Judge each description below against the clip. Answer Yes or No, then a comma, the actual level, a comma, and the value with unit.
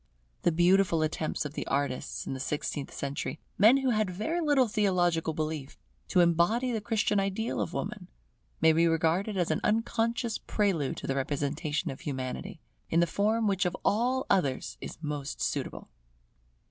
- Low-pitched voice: No, medium, 175 Hz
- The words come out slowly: No, average, 165 wpm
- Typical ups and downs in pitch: No, wide, 6.1 semitones